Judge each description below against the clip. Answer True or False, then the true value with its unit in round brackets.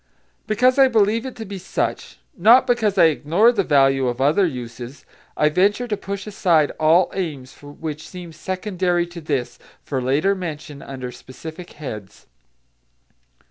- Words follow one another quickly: False (150 wpm)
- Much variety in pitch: True (5.8 semitones)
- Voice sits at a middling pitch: True (170 Hz)